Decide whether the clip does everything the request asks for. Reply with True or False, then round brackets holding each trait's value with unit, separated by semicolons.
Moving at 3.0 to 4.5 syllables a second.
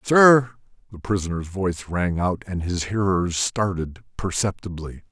True (4.4 syllables/s)